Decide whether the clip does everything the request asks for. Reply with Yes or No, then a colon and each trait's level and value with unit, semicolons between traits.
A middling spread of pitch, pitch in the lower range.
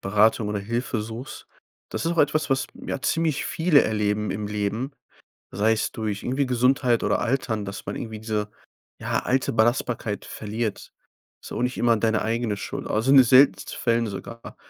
Yes: average, 3.5 semitones; low, 115 Hz